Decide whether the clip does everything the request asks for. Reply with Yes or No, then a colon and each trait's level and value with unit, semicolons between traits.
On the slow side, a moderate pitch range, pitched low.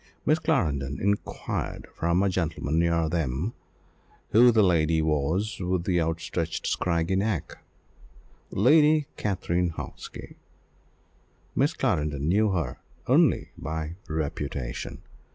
Yes: slow, 105 wpm; average, 4.2 semitones; very low, 85 Hz